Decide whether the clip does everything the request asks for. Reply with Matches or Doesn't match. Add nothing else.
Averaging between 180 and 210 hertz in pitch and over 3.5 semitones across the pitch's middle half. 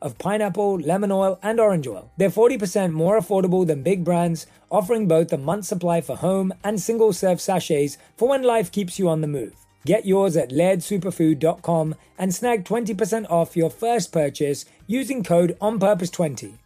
Matches